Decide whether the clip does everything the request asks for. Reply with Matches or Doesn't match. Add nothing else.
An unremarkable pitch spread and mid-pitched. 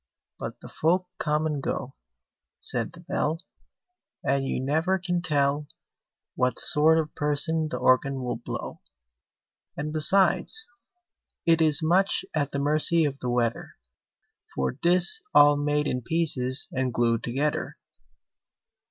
Matches